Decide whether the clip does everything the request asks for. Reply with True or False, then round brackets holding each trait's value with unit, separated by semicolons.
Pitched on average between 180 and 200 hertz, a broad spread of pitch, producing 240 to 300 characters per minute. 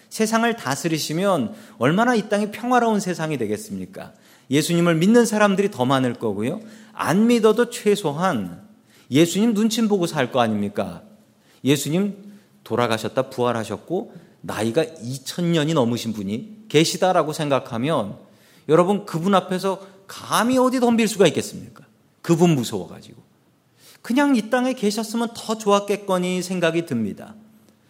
False (185 Hz; 7.7 semitones; 310 characters per minute)